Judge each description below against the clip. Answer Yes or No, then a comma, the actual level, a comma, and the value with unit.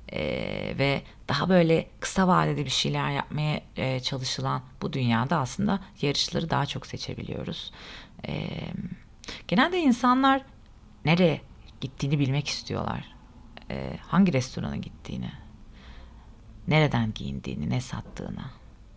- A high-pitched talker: No, medium, 140 Hz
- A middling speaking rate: Yes, average, 105 wpm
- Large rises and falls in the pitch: Yes, wide, 8.3 semitones